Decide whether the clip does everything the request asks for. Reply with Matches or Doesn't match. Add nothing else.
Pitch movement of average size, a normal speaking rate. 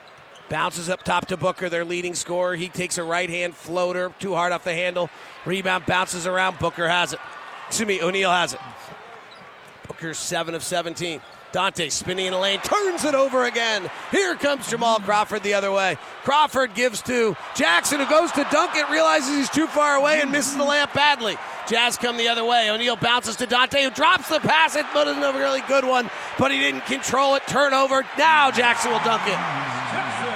Doesn't match